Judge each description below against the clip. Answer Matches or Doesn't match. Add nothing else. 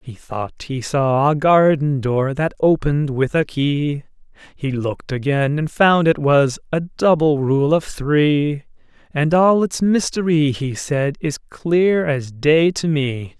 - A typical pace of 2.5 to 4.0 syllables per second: Matches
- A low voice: Doesn't match